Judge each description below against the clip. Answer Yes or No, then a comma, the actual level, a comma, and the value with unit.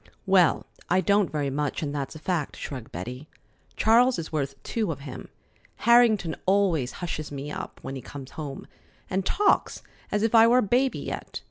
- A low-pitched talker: No, medium, 165 Hz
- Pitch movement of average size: No, wide, 6.8 semitones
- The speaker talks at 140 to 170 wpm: No, average, 180 wpm